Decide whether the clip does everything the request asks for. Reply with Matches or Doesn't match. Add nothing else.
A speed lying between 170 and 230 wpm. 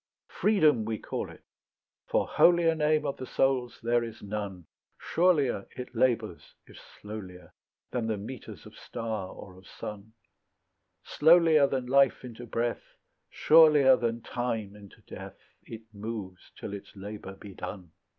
Doesn't match